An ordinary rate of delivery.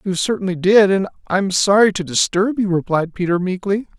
Yes: average, 180 wpm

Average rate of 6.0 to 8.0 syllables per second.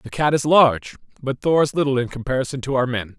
Yes: 6.3 syllables/s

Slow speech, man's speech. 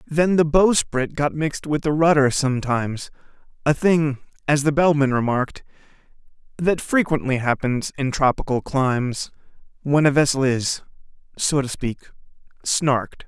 Yes: slow, 130 wpm; male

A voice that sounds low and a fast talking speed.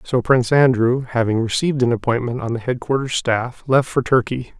No: low, 125 Hz; average, 185 wpm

